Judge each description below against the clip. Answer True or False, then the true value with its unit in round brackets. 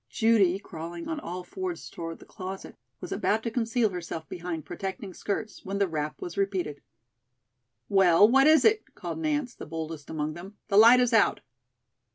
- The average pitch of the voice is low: False (195 Hz)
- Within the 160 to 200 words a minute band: True (175 wpm)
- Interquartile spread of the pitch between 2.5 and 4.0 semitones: False (5.4 semitones)